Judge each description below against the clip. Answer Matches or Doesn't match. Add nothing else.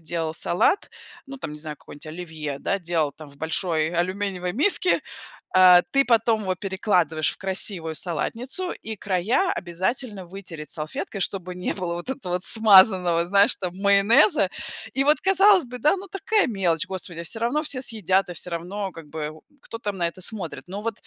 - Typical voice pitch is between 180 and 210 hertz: Matches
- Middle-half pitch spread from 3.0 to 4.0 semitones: Doesn't match